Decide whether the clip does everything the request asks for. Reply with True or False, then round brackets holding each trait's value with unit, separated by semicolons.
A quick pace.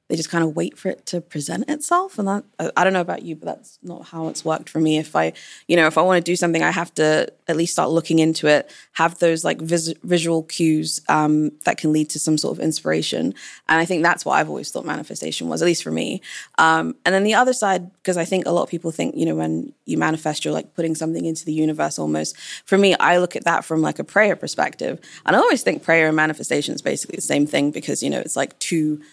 True (265 wpm)